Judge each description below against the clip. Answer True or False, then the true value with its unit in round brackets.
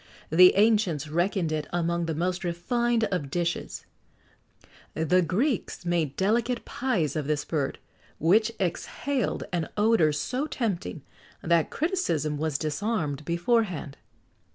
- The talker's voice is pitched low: False (175 Hz)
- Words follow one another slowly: True (125 wpm)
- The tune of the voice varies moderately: False (5.9 semitones)